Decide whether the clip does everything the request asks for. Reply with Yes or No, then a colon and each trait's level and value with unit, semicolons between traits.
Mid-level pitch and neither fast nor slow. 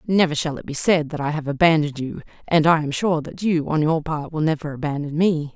No: medium, 155 Hz; fast, 250 wpm